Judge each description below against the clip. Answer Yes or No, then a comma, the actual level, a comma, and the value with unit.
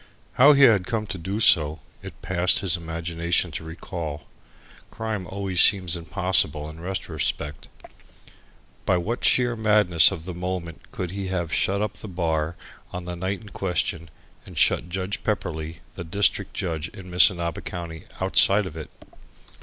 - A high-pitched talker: No, very low, 90 Hz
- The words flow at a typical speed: Yes, average, 155 wpm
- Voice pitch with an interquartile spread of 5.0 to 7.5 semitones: No, average, 3.0 semitones